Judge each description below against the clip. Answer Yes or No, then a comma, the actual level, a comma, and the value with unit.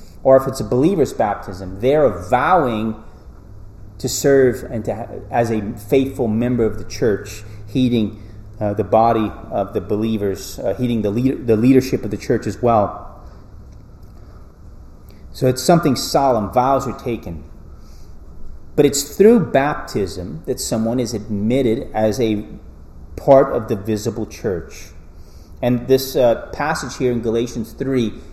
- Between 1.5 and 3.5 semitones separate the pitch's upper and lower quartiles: No, average, 4.1 semitones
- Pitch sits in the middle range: No, low, 110 Hz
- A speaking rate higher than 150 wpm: No, average, 140 wpm